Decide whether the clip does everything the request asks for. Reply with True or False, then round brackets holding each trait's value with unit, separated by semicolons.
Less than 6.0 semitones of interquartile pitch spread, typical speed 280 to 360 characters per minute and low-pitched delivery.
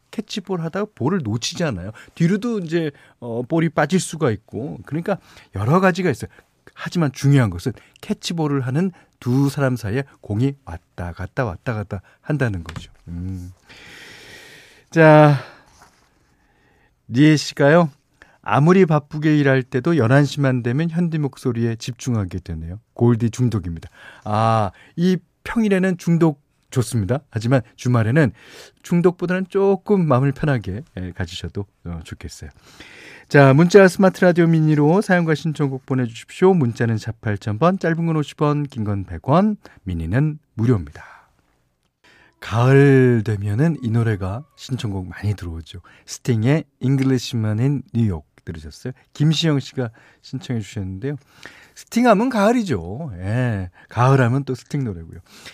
False (6.5 semitones; 285 characters per minute; 130 Hz)